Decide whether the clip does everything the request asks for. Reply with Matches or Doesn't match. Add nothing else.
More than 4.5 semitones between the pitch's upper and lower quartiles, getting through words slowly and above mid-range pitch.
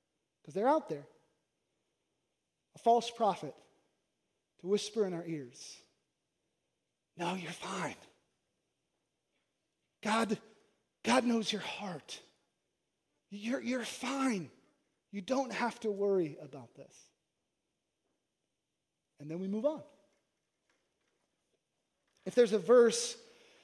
Matches